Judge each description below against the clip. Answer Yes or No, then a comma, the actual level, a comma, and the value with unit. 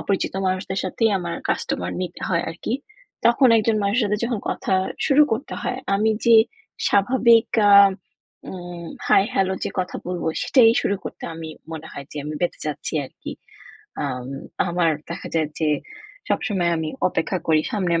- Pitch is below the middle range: No, high, 190 Hz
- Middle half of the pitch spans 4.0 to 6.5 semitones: Yes, average, 5.0 semitones